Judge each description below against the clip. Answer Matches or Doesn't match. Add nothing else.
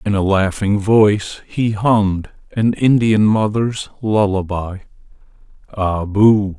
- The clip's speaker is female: Doesn't match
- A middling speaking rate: Doesn't match